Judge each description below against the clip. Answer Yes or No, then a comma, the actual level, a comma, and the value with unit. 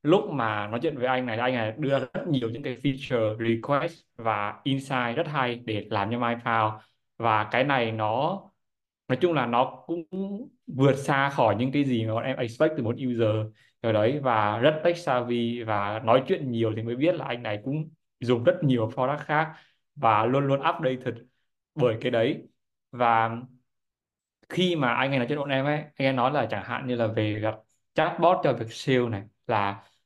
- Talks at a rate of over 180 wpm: Yes, average, 205 wpm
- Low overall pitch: Yes, low, 125 Hz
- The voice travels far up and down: No, average, 3.8 semitones